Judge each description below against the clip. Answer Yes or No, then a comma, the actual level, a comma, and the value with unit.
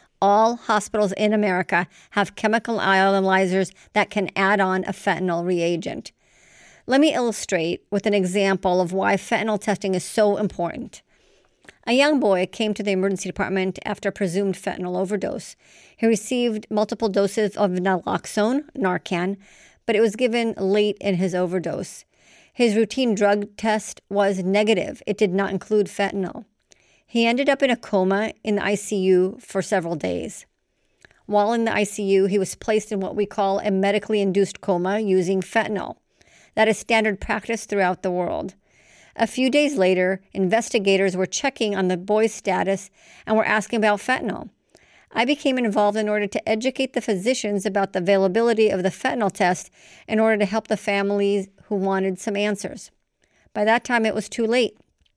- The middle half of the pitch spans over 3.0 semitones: No, narrow, 2.4 semitones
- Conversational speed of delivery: Yes, average, 165 wpm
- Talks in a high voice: Yes, high, 205 Hz